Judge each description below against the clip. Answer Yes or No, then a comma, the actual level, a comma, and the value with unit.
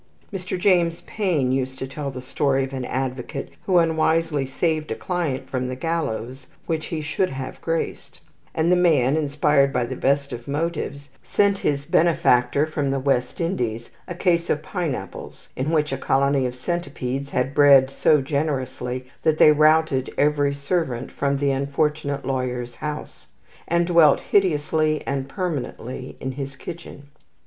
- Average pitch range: Yes, average, 3.4 semitones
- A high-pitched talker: No, medium, 140 Hz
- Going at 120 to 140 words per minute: No, average, 155 wpm